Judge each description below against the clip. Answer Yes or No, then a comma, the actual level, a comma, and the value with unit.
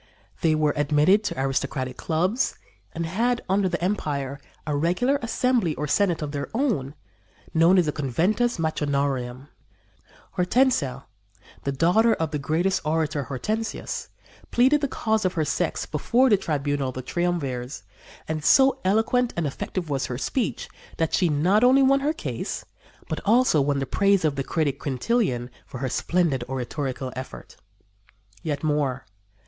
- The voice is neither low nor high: Yes, medium, 160 Hz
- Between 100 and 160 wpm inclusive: Yes, average, 155 wpm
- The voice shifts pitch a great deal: Yes, wide, 6.7 semitones